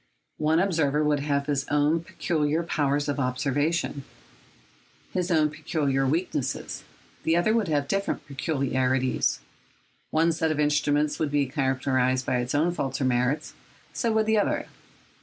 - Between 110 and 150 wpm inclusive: Yes, average, 145 wpm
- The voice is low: No, medium, 145 Hz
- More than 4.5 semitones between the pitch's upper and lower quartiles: No, average, 3.1 semitones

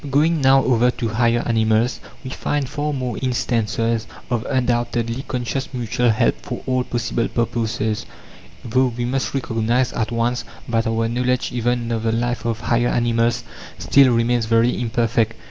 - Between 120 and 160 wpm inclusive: Yes, average, 155 wpm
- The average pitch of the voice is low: Yes, low, 120 Hz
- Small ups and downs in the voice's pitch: Yes, narrow, 1.6 semitones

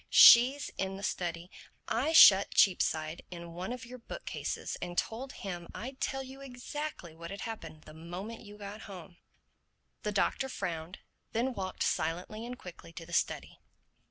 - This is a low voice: No, high, 195 Hz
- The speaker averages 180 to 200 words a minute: No, average, 165 wpm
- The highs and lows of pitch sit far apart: Yes, wide, 6.2 semitones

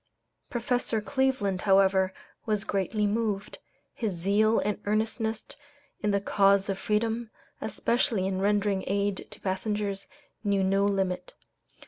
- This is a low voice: No, high, 205 Hz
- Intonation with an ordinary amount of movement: No, narrow, 2.0 semitones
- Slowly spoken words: Yes, slow, 120 wpm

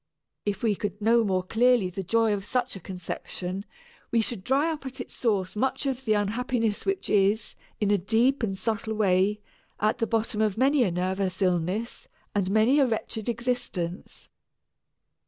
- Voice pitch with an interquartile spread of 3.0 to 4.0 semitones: Yes, average, 3.7 semitones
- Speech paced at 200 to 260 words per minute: No, average, 175 wpm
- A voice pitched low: No, high, 215 Hz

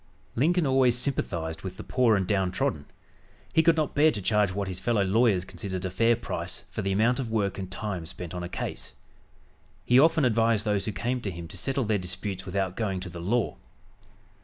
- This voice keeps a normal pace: No, fast, 210 wpm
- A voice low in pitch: Yes, low, 100 Hz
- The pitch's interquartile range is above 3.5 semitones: Yes, average, 4.5 semitones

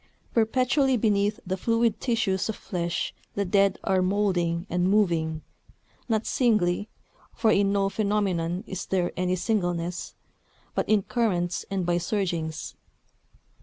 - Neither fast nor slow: No, slow, 130 wpm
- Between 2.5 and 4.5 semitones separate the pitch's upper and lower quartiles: Yes, average, 3.3 semitones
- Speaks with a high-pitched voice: Yes, high, 195 Hz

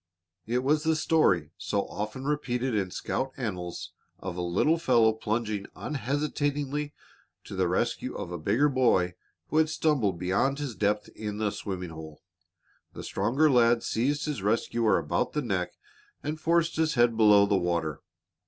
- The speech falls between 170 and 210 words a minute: No, average, 160 wpm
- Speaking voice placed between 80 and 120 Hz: Yes, low, 115 Hz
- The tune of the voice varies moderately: No, wide, 6.6 semitones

